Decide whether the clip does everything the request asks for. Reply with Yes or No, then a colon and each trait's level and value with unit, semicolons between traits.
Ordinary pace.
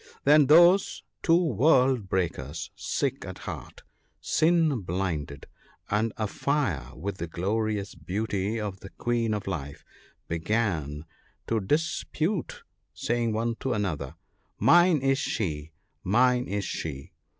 No: slow, 125 wpm